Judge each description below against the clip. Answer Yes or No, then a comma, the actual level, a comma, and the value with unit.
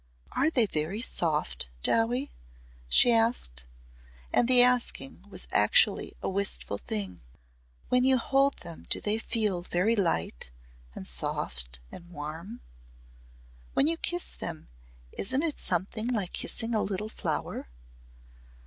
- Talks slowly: Yes, slow, 130 wpm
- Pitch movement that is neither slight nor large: No, wide, 7.3 semitones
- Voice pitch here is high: Yes, high, 210 Hz